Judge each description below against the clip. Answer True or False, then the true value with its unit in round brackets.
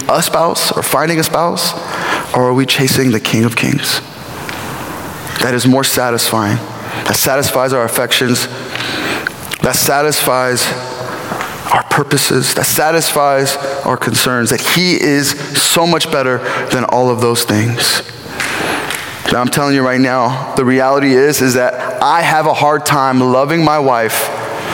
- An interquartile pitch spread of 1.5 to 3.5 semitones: True (2.5 semitones)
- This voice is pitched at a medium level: False (130 Hz)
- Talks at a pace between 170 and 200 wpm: False (145 wpm)